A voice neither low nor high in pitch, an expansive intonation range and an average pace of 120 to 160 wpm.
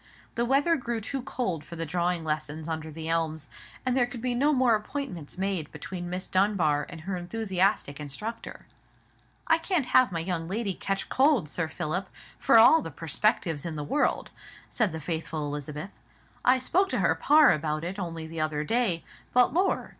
No: medium, 180 Hz; wide, 7.2 semitones; average, 185 wpm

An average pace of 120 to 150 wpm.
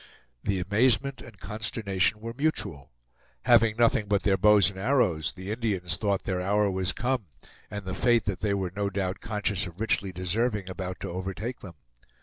No: average, 175 wpm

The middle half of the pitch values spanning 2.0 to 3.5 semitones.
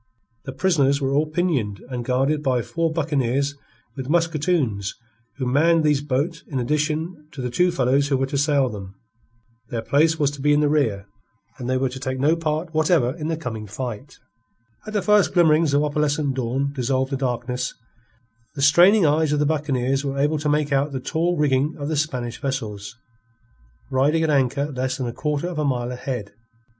Yes: average, 3.1 semitones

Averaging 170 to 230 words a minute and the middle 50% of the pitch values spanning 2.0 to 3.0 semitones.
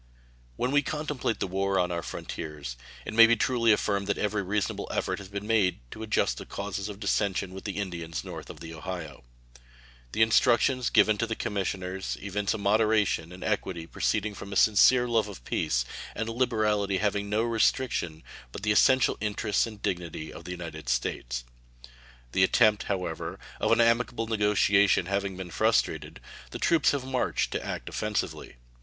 No: average, 175 wpm; average, 3.4 semitones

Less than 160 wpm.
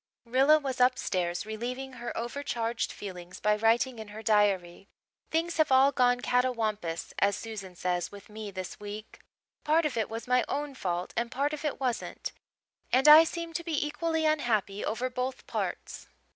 No: average, 170 wpm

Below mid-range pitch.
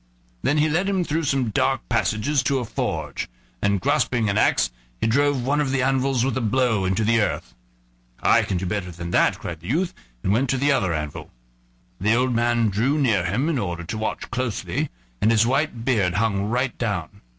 Yes: low, 120 Hz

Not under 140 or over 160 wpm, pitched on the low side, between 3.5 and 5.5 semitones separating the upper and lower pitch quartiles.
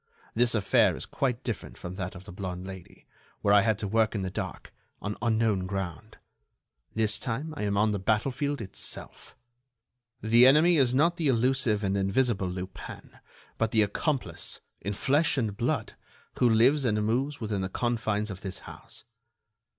No: average, 170 wpm; low, 110 Hz; average, 4.1 semitones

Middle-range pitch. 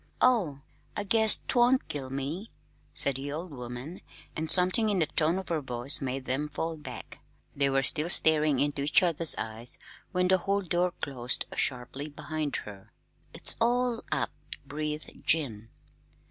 Yes: medium, 150 Hz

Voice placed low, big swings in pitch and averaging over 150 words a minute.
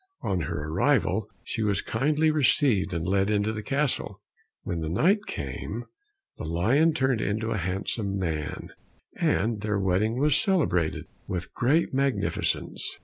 No: low, 105 Hz; wide, 6.5 semitones; average, 140 wpm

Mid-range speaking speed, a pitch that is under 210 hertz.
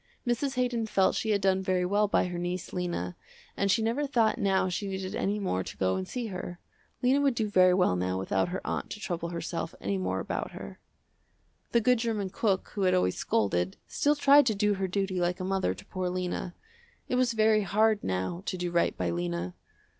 No: fast, 215 wpm; high, 190 Hz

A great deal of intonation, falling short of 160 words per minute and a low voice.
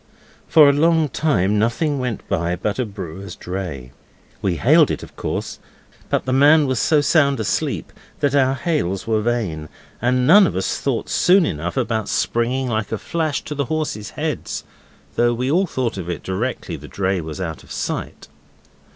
No: wide, 6.9 semitones; average, 180 wpm; low, 120 Hz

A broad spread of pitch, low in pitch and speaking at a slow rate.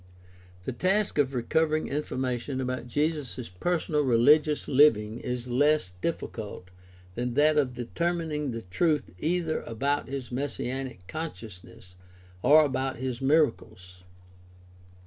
No: average, 4.3 semitones; low, 130 Hz; slow, 115 wpm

